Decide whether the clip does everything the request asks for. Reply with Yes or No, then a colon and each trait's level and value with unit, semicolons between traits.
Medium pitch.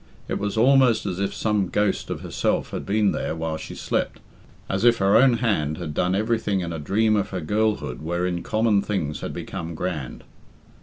No: low, 100 Hz